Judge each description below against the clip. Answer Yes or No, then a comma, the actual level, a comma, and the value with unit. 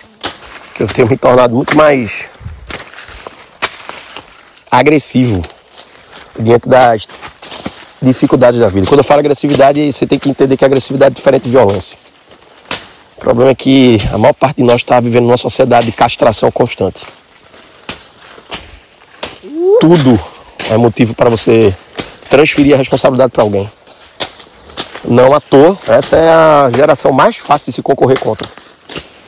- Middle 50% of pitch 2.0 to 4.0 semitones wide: Yes, average, 2.7 semitones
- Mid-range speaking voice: No, low, 130 Hz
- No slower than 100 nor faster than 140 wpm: Yes, average, 135 wpm